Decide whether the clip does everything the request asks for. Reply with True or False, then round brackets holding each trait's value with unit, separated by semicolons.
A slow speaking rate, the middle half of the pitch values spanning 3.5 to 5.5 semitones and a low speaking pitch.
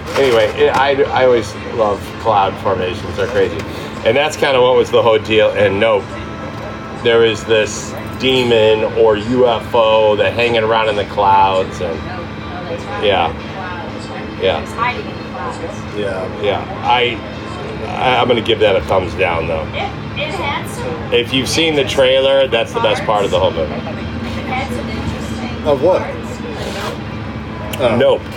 True (130 wpm; 4.9 semitones; 110 Hz)